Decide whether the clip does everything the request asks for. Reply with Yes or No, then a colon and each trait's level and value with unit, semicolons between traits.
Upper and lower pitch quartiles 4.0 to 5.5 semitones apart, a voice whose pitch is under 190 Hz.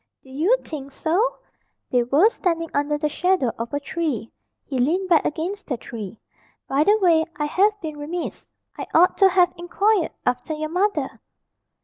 No: average, 4.4 semitones; very high, 320 Hz